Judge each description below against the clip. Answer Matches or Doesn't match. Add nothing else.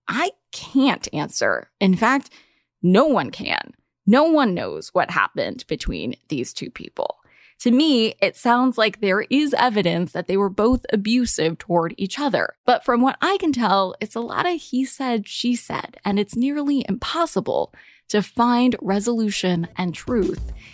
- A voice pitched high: Matches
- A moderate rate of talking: Matches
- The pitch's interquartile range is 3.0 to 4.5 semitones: Doesn't match